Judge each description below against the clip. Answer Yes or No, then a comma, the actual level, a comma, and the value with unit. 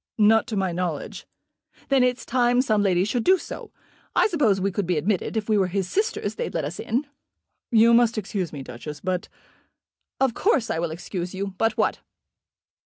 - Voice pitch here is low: No, high, 210 Hz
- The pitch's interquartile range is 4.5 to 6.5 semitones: Yes, average, 4.9 semitones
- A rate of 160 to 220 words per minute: Yes, average, 195 wpm